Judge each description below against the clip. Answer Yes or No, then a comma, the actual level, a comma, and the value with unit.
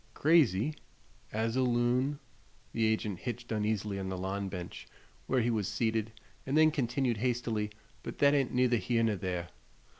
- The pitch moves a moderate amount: Yes, average, 3.2 semitones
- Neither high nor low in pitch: No, low, 115 Hz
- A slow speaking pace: No, average, 160 wpm